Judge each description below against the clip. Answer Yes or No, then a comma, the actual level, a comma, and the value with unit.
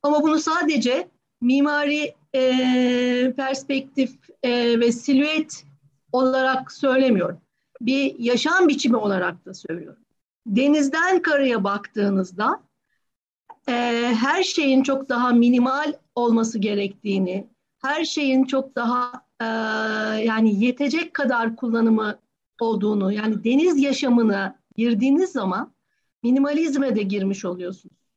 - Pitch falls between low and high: No, high, 245 Hz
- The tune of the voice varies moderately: Yes, average, 4.0 semitones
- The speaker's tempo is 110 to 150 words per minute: No, average, 100 wpm